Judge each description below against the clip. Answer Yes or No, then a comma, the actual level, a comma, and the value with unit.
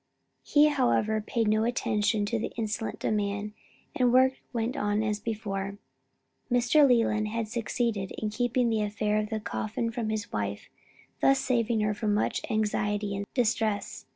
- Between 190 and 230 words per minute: No, average, 155 wpm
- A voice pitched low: No, high, 215 Hz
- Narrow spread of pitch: Yes, narrow, 2.0 semitones